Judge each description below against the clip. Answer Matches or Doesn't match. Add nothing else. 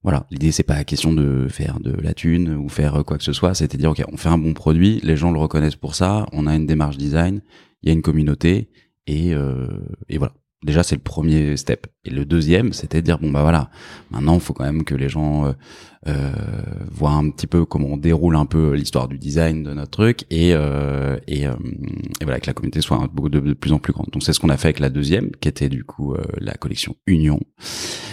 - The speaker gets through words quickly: Matches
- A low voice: Matches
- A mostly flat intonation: Matches